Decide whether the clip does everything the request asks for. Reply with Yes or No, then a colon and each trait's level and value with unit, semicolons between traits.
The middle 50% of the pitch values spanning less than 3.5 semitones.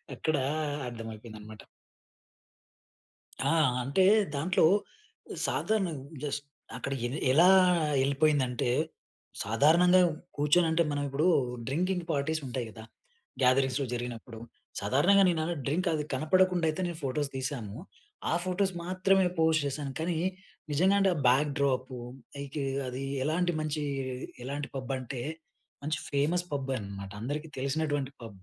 No: average, 4.3 semitones